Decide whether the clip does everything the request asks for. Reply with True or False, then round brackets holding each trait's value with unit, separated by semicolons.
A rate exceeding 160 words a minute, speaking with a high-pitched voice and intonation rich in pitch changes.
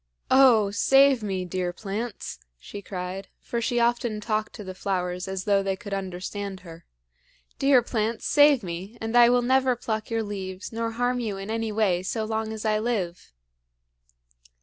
False (170 wpm; 215 Hz; 3.7 semitones)